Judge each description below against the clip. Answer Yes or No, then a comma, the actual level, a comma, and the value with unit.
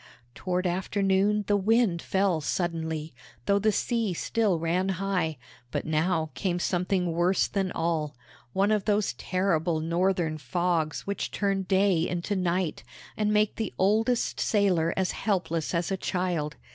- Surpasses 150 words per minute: No, average, 145 wpm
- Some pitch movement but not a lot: Yes, average, 3.2 semitones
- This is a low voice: No, medium, 185 Hz